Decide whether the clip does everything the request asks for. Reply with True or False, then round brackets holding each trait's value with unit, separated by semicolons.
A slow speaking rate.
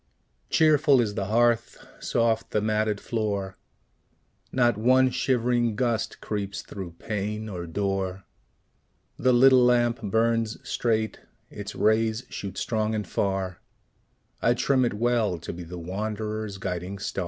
True (130 wpm)